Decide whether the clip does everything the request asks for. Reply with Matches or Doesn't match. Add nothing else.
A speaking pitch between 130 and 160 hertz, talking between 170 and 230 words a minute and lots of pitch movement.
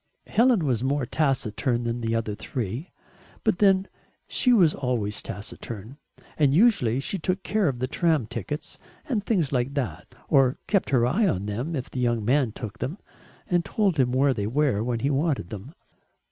Matches